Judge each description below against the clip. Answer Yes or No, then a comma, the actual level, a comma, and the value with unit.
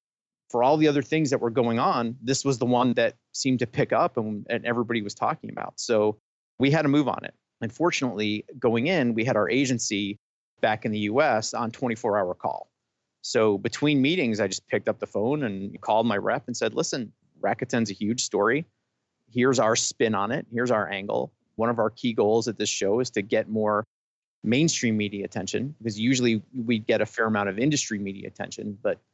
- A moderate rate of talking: No, fast, 210 wpm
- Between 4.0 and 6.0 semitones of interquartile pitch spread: No, average, 3.6 semitones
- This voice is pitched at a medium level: No, low, 115 Hz